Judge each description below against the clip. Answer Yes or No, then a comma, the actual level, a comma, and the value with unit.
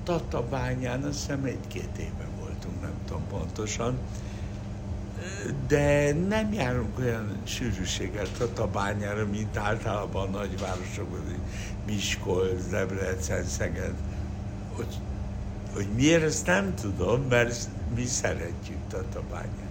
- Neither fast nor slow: No, slow, 100 wpm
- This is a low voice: Yes, low, 100 Hz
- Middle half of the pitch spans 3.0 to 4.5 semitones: No, narrow, 2.6 semitones